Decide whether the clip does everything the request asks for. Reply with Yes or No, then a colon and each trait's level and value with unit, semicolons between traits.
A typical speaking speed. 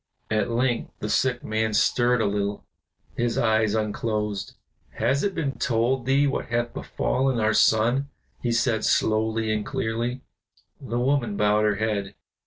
Yes: average, 150 wpm